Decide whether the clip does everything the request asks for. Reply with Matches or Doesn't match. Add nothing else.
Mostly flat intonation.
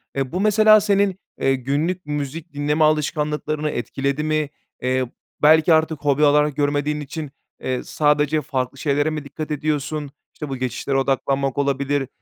Matches